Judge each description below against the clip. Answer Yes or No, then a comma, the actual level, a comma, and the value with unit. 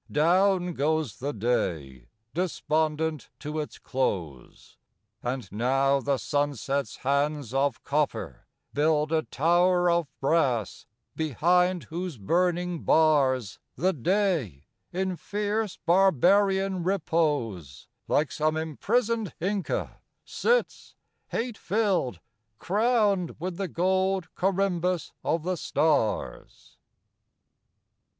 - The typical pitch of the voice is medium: Yes, medium, 160 Hz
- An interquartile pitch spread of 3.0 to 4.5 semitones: No, average, 5.0 semitones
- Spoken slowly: Yes, slow, 95 wpm